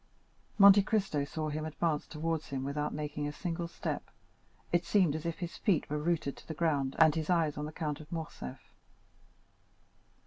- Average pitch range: No, narrow, 2.3 semitones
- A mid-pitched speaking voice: Yes, medium, 155 Hz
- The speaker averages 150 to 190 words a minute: Yes, average, 180 wpm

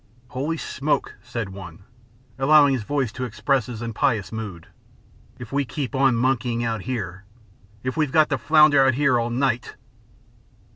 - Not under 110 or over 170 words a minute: Yes, average, 155 wpm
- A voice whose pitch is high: No, low, 125 Hz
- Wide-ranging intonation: No, average, 3.6 semitones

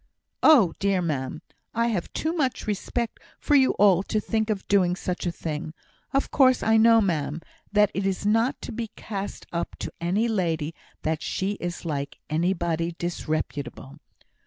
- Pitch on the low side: No, high, 190 Hz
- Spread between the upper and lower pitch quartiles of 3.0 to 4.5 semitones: No, average, 4.9 semitones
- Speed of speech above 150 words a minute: Yes, average, 165 wpm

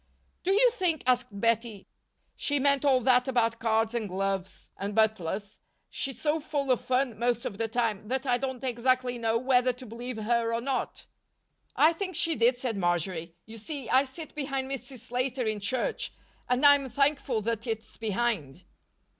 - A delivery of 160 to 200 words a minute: Yes, average, 175 wpm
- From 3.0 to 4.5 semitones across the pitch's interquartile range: Yes, average, 3.3 semitones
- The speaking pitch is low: No, high, 245 Hz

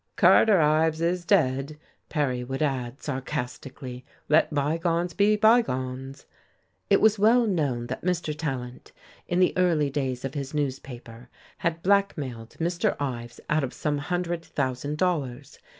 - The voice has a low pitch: No, medium, 150 Hz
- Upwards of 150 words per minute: No, slow, 135 wpm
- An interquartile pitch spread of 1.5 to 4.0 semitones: No, average, 4.9 semitones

